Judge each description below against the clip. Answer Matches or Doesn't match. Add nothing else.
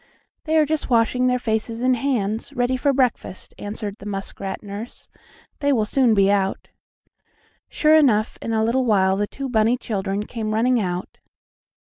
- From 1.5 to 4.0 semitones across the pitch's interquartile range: Matches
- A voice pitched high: Matches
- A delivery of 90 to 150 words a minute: Doesn't match